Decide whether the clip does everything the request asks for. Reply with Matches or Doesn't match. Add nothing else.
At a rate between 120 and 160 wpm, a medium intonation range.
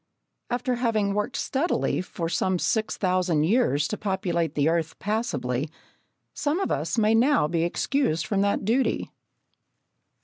Doesn't match